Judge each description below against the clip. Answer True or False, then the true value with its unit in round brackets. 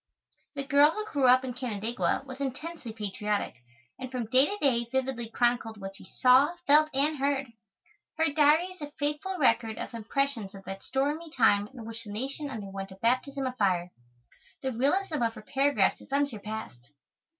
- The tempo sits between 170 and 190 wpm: True (175 wpm)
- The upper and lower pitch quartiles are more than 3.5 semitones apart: True (4.5 semitones)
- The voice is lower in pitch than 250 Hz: False (255 Hz)